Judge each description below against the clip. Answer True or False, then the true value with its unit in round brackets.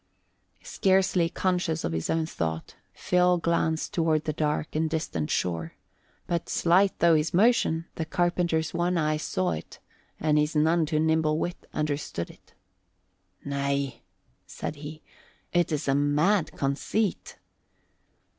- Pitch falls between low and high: True (160 Hz)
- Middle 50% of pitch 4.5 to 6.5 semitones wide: False (2.7 semitones)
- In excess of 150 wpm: False (135 wpm)